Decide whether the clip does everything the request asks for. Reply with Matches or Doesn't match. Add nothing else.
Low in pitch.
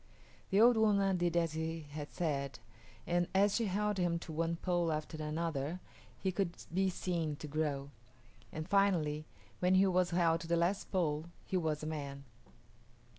Doesn't match